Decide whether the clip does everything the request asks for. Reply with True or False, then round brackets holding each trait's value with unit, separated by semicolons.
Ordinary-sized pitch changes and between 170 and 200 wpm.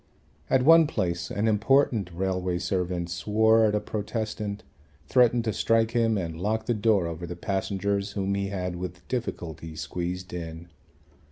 False (4.0 semitones; 155 wpm)